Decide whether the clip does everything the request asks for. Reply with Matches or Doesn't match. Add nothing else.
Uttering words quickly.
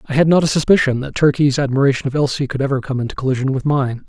Matches